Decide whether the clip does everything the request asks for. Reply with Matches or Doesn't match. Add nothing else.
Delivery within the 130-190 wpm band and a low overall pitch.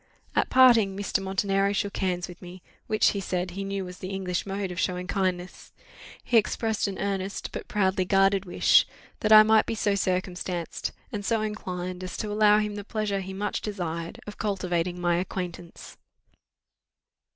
Doesn't match